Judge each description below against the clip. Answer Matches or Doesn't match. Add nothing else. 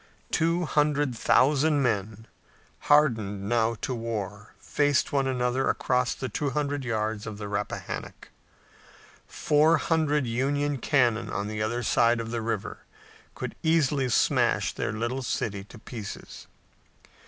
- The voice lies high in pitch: Doesn't match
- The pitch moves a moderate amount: Matches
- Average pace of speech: Doesn't match